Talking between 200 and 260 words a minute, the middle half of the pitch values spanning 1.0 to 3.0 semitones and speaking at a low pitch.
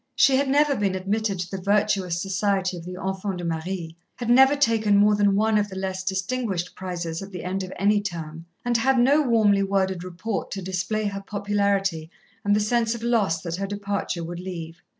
No: fast, 205 wpm; average, 2.7 semitones; high, 195 Hz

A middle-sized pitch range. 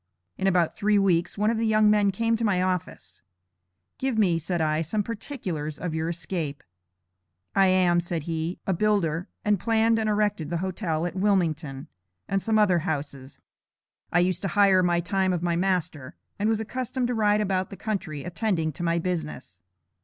Yes: average, 4.0 semitones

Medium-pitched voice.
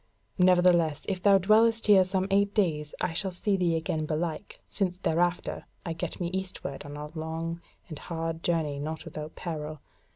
Yes: medium, 170 Hz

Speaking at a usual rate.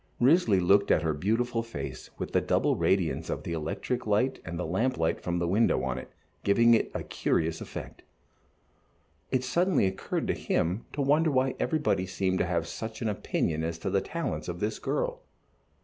Yes: average, 190 wpm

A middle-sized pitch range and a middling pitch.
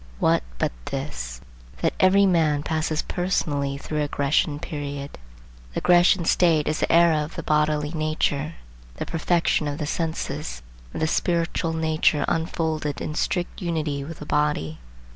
No: narrow, 2.2 semitones; medium, 155 Hz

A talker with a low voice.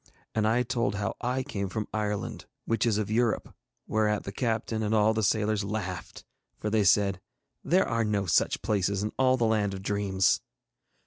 Yes: low, 105 Hz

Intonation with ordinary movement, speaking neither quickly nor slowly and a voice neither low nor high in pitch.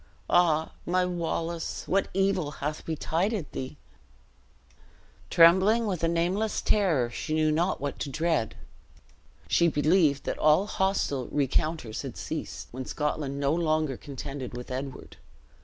No: average, 3.9 semitones; slow, 130 wpm; medium, 160 Hz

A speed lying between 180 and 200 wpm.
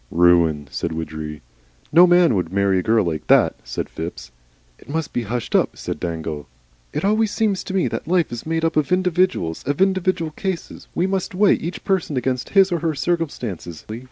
Yes: average, 190 wpm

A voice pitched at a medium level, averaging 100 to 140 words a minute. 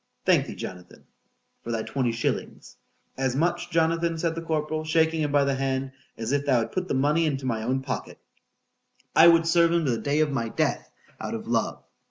No: medium, 145 Hz; average, 200 wpm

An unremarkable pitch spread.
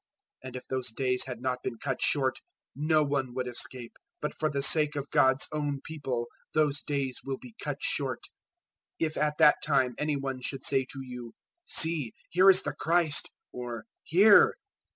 Yes: average, 3.0 semitones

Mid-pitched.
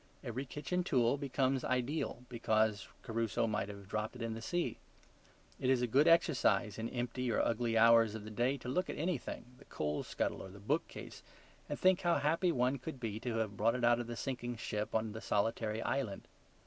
No: low, 120 Hz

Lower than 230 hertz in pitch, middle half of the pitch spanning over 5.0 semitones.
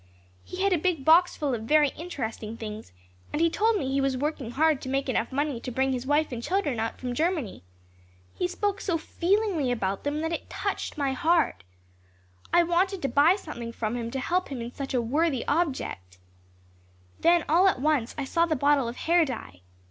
No: very high, 290 Hz; wide, 5.4 semitones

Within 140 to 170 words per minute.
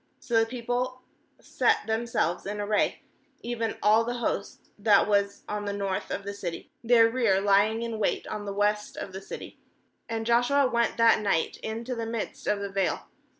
No: average, 185 wpm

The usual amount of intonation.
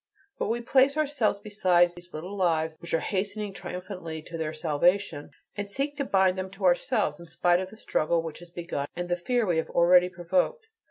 Yes: average, 3.3 semitones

